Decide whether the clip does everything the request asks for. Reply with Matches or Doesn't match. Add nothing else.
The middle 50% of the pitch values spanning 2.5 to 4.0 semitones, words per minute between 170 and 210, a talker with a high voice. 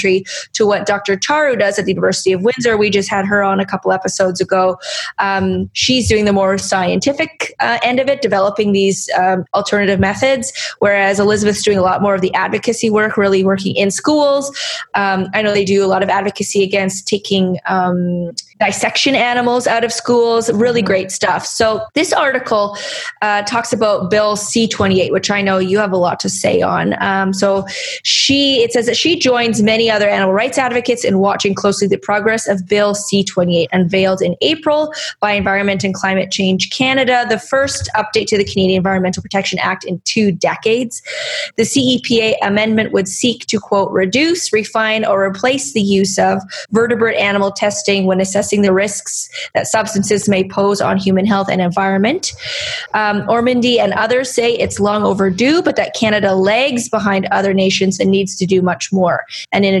Matches